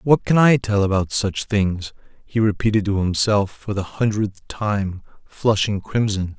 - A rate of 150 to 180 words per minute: Yes, average, 160 wpm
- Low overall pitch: Yes, low, 105 Hz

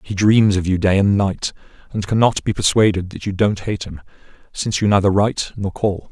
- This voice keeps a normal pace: No, fast, 215 wpm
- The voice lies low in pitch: Yes, low, 100 Hz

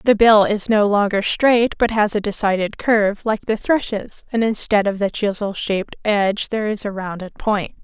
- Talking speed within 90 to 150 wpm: No, average, 200 wpm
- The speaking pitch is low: No, high, 210 Hz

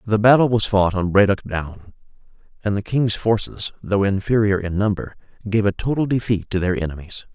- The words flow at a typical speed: Yes, average, 180 wpm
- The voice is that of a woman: No, male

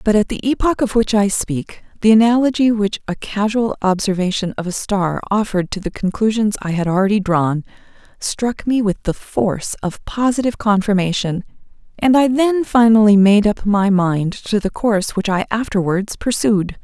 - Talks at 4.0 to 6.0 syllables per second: Yes, 5.0 syllables/s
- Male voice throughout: No, female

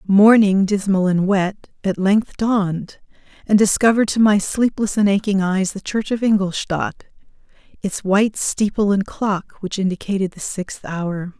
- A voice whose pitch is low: No, high, 200 Hz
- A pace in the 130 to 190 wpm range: Yes, average, 155 wpm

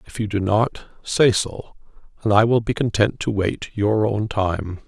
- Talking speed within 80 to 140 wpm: No, average, 195 wpm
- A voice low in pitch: Yes, low, 105 Hz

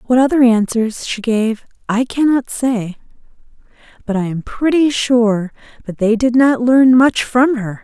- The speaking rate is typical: Yes, average, 160 wpm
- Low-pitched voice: No, high, 240 Hz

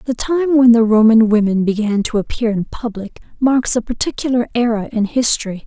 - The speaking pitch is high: Yes, high, 230 Hz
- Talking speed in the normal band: Yes, average, 180 wpm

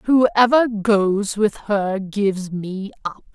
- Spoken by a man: No, female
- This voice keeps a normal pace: No, slow, 125 wpm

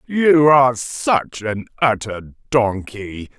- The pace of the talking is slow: Yes, slow, 105 wpm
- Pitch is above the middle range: No, low, 120 Hz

